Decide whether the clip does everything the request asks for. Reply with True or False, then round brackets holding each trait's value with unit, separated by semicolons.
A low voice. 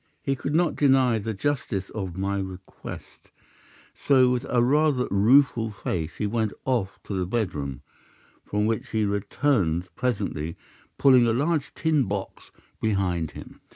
True (110 Hz)